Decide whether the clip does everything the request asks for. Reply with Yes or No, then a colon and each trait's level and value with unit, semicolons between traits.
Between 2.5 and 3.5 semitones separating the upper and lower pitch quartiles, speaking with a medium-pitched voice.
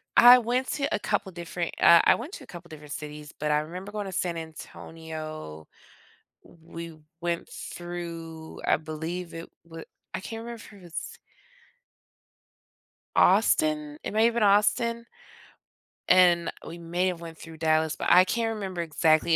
No: average, 4.2 semitones; medium, 170 Hz